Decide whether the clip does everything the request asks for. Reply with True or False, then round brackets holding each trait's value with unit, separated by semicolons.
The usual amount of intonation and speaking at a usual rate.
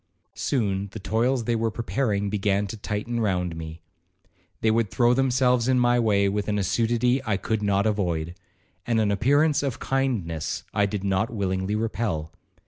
True (3.4 semitones; 165 wpm)